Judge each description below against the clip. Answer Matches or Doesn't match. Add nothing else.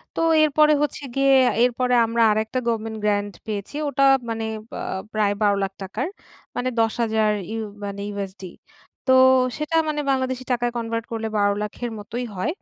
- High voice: Matches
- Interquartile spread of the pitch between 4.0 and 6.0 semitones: Doesn't match